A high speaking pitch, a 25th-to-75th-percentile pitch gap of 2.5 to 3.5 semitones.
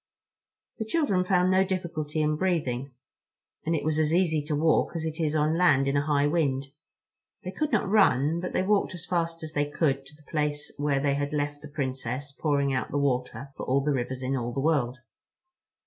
No: medium, 150 Hz; average, 3.2 semitones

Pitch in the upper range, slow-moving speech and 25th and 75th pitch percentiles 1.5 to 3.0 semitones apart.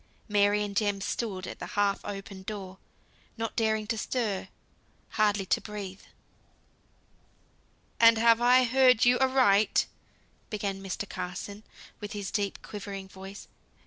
Yes: high, 205 Hz; slow, 130 wpm; narrow, 2.4 semitones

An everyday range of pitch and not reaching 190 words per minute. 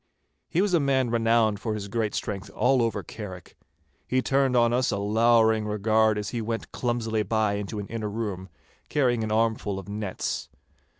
No: narrow, 2.2 semitones; average, 180 wpm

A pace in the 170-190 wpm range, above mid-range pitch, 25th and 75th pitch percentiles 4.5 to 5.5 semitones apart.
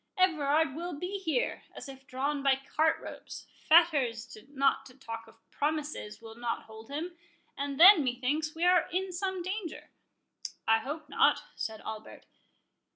No: average, 150 wpm; very high, 290 Hz; average, 5.2 semitones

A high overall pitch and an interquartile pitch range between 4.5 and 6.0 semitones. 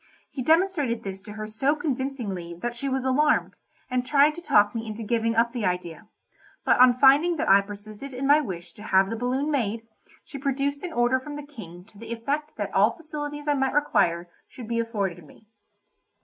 Yes: high, 245 Hz; average, 5.3 semitones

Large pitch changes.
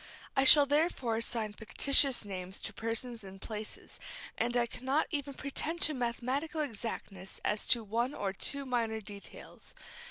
No: average, 4.4 semitones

